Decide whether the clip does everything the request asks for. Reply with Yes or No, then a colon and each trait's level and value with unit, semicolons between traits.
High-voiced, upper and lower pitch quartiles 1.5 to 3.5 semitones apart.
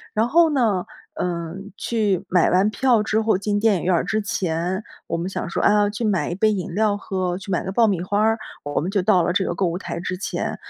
Yes: high, 195 Hz; average, 3.1 semitones